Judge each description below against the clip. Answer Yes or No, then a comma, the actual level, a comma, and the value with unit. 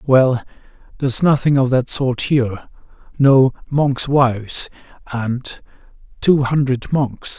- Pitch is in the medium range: No, low, 130 Hz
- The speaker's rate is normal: No, slow, 115 wpm